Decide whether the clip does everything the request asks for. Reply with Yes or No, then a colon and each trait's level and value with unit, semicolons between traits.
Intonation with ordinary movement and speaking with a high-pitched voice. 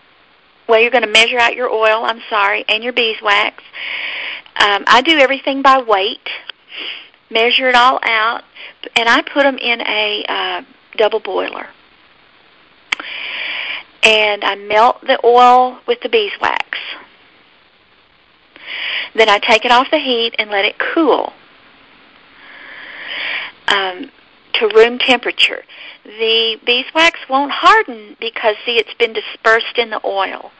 No: wide, 6.7 semitones; high, 245 Hz